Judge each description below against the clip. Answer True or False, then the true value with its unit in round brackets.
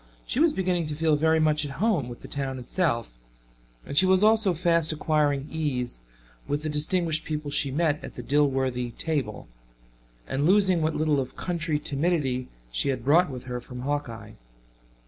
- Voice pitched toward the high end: False (150 Hz)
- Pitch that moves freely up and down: False (3.8 semitones)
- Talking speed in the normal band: True (175 wpm)